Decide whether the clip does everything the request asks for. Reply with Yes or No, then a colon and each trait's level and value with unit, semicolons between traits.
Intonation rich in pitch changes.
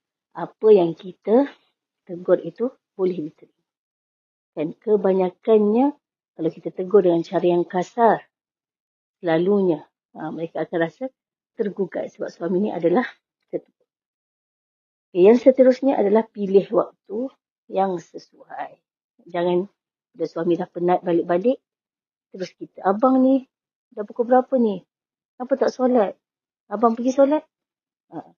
Yes: wide, 6.4 semitones